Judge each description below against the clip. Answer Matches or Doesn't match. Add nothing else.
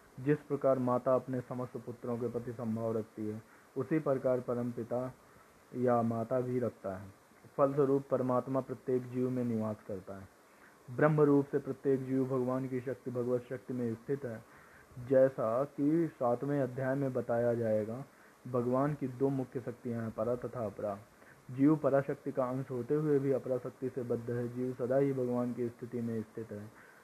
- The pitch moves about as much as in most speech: Doesn't match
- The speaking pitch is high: Doesn't match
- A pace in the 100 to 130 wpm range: Doesn't match